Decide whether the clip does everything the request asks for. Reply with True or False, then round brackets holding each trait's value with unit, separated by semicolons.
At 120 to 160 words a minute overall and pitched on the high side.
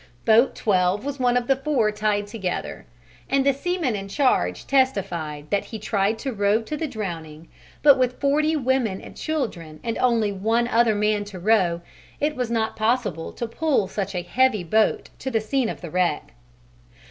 False (180 wpm; 220 Hz)